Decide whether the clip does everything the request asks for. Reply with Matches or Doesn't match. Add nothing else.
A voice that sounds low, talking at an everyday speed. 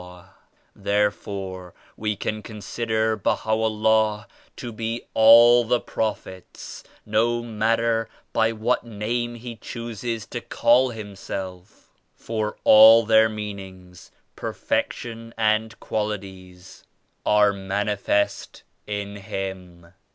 Doesn't match